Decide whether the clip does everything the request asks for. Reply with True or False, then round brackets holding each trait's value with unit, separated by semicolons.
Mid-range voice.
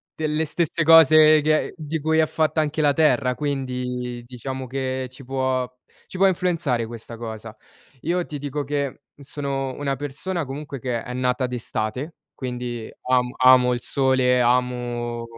False (130 Hz)